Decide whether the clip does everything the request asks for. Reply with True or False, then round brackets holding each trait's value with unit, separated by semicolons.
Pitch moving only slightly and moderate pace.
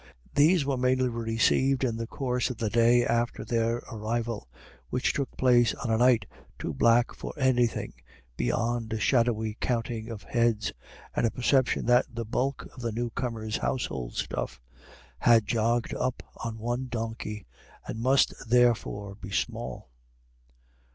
True (1.8 semitones; 150 wpm)